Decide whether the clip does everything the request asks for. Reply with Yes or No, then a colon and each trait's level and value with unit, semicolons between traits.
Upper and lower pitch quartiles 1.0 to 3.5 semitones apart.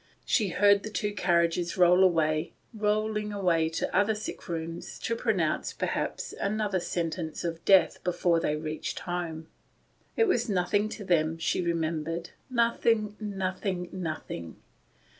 No: average, 4.0 semitones